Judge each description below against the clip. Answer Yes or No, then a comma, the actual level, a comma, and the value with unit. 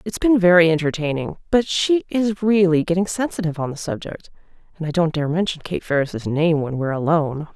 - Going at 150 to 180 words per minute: No, average, 190 wpm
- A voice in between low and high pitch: Yes, medium, 170 Hz